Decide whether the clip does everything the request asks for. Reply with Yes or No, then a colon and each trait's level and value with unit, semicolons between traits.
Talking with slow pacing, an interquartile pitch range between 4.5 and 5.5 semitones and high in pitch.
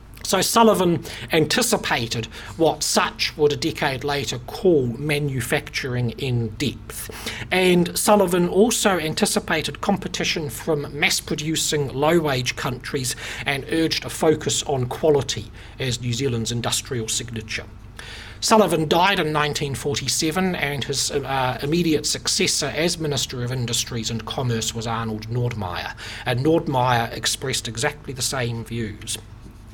No: slow, 120 wpm; average, 5.2 semitones; low, 135 Hz